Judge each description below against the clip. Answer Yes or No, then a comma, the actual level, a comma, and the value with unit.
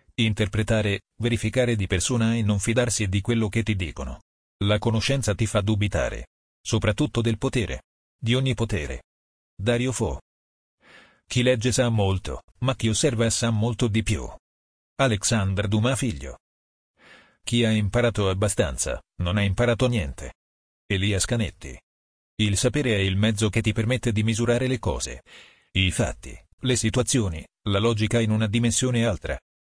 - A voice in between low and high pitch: No, low, 110 Hz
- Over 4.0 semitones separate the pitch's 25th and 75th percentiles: Yes, average, 4.6 semitones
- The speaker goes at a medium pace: Yes, average, 145 wpm